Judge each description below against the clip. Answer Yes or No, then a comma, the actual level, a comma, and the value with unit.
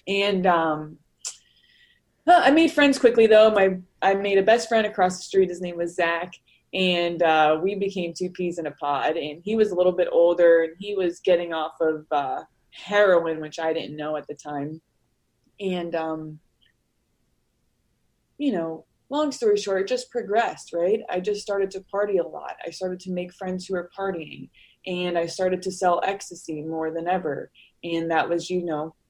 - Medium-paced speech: Yes, average, 190 wpm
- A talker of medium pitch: Yes, medium, 180 Hz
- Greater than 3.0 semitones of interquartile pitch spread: Yes, average, 3.5 semitones